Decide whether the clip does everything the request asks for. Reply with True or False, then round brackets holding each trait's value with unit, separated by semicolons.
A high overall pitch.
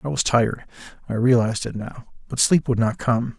False (120 Hz)